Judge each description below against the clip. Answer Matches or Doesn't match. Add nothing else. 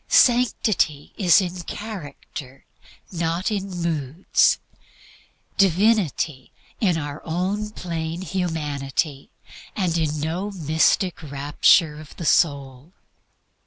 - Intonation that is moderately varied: Matches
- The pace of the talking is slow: Matches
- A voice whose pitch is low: Doesn't match